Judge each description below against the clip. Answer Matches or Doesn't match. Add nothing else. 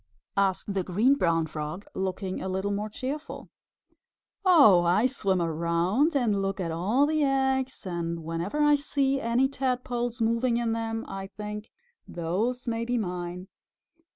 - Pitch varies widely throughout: Matches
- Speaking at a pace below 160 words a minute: Matches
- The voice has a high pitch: Matches